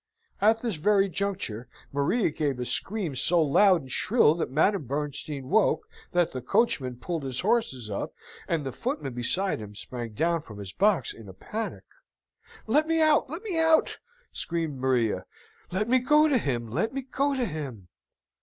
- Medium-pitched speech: Yes, medium, 165 Hz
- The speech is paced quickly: No, average, 175 wpm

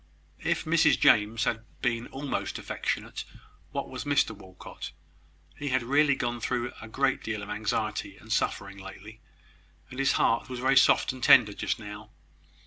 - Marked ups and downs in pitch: No, average, 3.8 semitones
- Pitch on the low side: Yes, low, 115 Hz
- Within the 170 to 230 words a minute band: No, average, 160 wpm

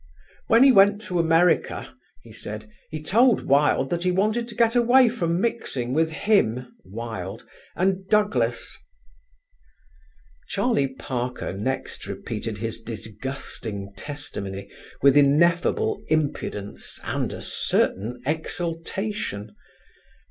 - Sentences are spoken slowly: Yes, slow, 110 wpm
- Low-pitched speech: No, medium, 155 Hz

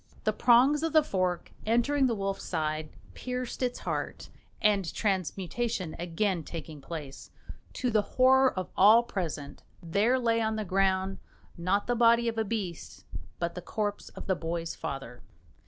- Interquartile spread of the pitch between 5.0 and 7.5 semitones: Yes, wide, 5.5 semitones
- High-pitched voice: Yes, high, 200 Hz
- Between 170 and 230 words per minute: No, average, 155 wpm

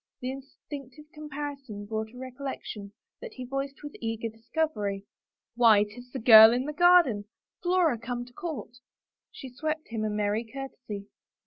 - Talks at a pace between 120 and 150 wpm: No, average, 175 wpm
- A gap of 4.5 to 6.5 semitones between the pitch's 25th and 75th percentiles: Yes, average, 4.8 semitones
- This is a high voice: Yes, very high, 250 Hz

